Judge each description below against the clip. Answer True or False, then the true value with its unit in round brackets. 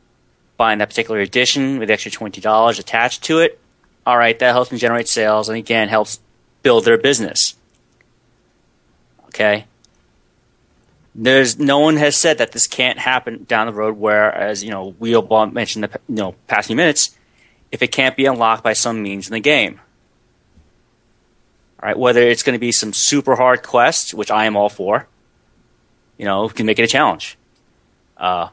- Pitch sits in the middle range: False (115 Hz)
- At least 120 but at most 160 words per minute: False (180 wpm)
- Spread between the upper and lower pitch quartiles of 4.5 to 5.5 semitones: False (2.9 semitones)